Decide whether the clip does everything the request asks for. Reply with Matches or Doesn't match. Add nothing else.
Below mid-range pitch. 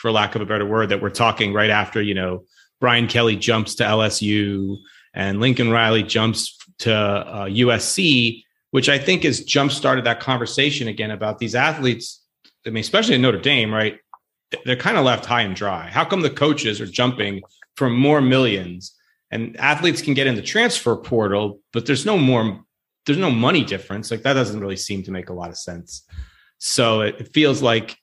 Matches